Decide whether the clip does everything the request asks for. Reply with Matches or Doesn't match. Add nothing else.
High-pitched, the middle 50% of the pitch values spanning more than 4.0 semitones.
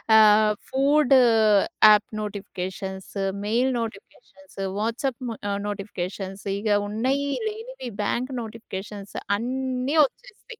Matches